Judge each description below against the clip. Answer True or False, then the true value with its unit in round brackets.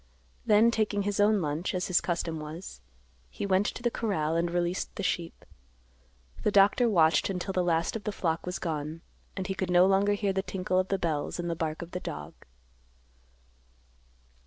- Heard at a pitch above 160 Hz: True (185 Hz)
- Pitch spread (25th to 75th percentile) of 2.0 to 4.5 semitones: True (3.2 semitones)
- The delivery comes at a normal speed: True (190 wpm)